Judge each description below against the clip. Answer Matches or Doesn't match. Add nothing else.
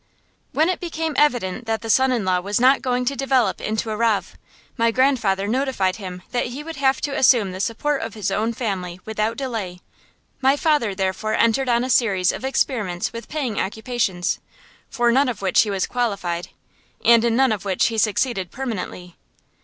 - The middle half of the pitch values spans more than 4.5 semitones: Matches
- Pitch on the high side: Matches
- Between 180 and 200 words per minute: Matches